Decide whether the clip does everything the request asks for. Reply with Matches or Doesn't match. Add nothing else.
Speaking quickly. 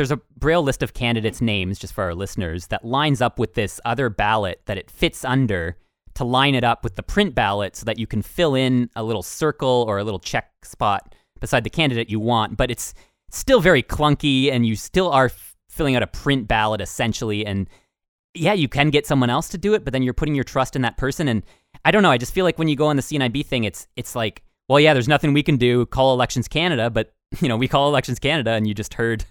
Matches